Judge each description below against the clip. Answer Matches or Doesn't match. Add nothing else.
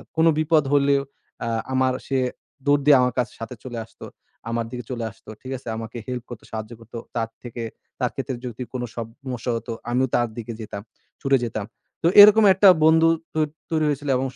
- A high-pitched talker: Doesn't match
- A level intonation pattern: Doesn't match